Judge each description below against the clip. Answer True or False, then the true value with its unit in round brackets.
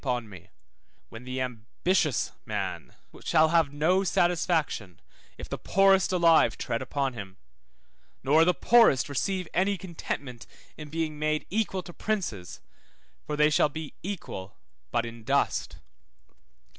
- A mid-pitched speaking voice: True (150 Hz)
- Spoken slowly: True (130 wpm)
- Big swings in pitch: True (6.1 semitones)